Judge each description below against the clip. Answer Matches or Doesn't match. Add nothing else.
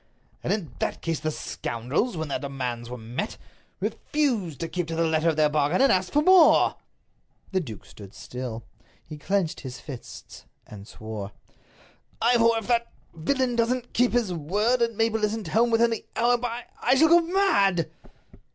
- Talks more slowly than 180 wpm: Matches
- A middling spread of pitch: Doesn't match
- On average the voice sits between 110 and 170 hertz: Doesn't match